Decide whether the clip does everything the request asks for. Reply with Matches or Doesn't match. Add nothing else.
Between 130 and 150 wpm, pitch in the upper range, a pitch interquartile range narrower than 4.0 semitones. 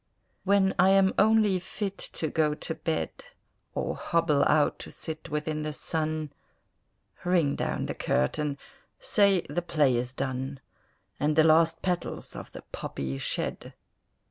Doesn't match